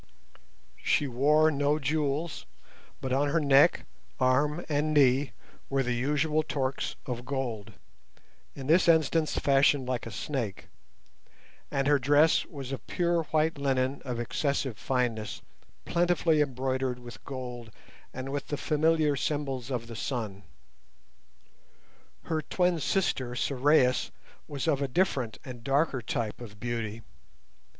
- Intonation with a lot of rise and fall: No, average, 3.2 semitones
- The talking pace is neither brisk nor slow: No, slow, 130 wpm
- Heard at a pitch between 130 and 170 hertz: Yes, low, 135 Hz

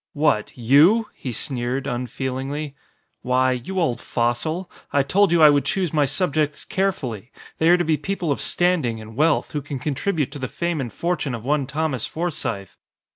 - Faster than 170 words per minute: Yes, average, 180 wpm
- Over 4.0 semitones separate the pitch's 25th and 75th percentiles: Yes, average, 4.5 semitones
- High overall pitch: No, medium, 145 Hz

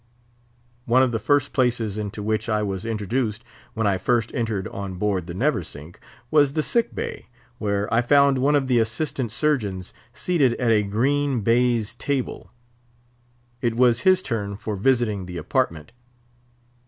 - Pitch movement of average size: Yes, average, 4.3 semitones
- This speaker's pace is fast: No, average, 155 wpm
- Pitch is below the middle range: Yes, low, 115 Hz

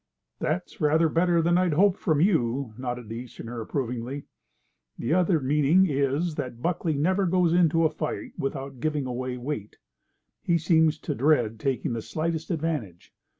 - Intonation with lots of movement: No, average, 4.8 semitones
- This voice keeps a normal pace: Yes, average, 155 wpm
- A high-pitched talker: No, medium, 150 Hz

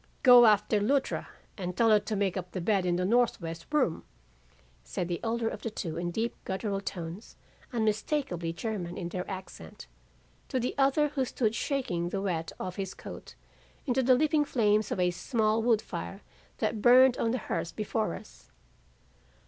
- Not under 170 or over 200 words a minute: Yes, average, 175 wpm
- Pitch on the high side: Yes, high, 210 Hz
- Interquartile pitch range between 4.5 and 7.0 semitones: Yes, average, 5.1 semitones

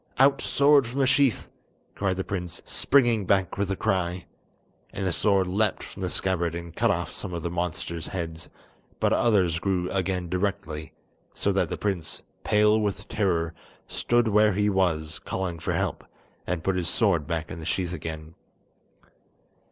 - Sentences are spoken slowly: No, average, 170 wpm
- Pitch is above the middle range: No, very low, 95 Hz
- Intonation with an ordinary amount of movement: Yes, average, 3.5 semitones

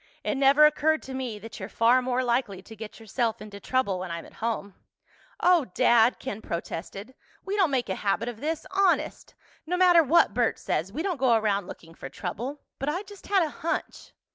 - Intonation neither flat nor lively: No, wide, 6.4 semitones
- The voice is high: Yes, high, 245 Hz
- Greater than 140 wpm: Yes, average, 200 wpm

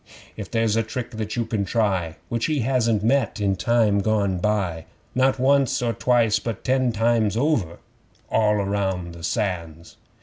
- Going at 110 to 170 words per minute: Yes, average, 165 wpm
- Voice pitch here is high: No, low, 110 Hz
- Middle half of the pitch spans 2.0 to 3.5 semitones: Yes, average, 3.2 semitones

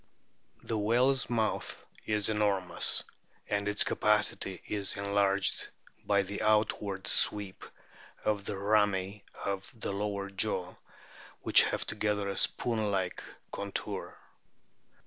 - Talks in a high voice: No, low, 100 Hz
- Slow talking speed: Yes, slow, 110 wpm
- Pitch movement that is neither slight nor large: No, narrow, 1.4 semitones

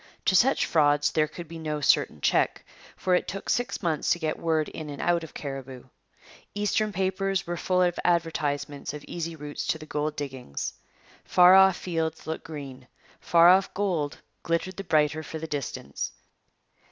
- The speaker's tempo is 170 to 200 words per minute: Yes, average, 175 wpm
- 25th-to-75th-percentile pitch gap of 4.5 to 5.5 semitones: No, average, 3.4 semitones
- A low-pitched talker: No, medium, 160 Hz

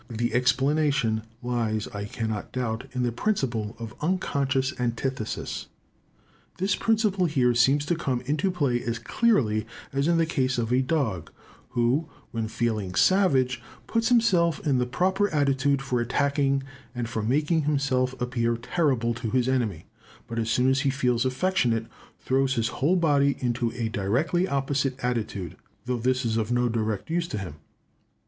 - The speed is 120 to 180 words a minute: Yes, average, 160 wpm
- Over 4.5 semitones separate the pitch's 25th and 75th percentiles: No, average, 3.7 semitones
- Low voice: Yes, low, 130 Hz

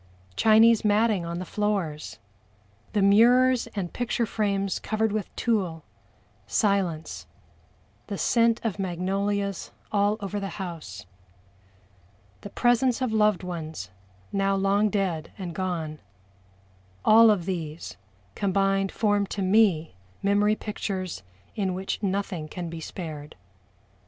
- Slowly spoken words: Yes, slow, 115 wpm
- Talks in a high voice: Yes, high, 195 Hz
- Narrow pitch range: No, average, 3.2 semitones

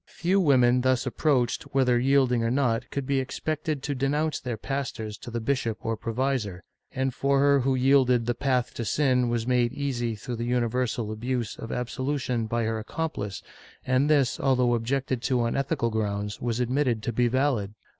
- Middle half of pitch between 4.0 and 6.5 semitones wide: No, average, 2.8 semitones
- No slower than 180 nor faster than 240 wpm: Yes, average, 185 wpm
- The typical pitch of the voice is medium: No, low, 125 Hz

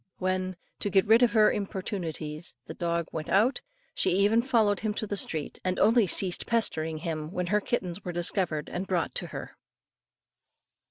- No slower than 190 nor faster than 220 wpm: No, average, 175 wpm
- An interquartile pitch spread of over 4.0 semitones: No, average, 3.6 semitones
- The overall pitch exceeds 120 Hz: Yes, medium, 185 Hz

